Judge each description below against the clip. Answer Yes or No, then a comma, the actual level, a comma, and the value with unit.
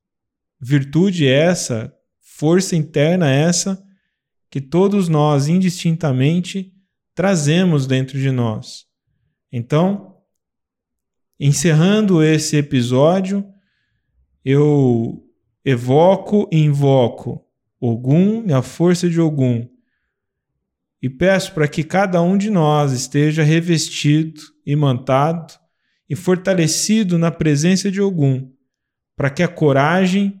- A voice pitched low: No, medium, 155 Hz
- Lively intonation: No, average, 5.0 semitones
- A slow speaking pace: Yes, slow, 95 wpm